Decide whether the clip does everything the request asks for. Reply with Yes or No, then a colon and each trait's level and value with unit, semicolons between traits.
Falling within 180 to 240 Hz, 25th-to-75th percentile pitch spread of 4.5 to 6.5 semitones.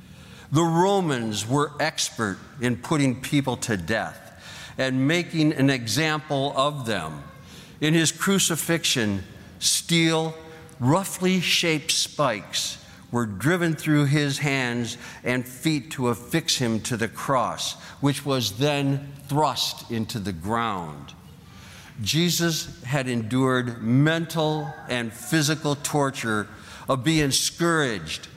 No: medium, 140 Hz; average, 4.9 semitones